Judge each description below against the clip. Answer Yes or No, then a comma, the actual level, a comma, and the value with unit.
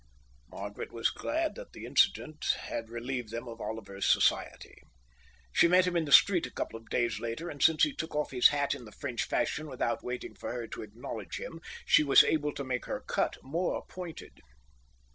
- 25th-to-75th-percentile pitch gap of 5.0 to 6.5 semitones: Yes, wide, 5.6 semitones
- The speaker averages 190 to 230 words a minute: Yes, average, 200 wpm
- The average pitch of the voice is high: No, low, 130 Hz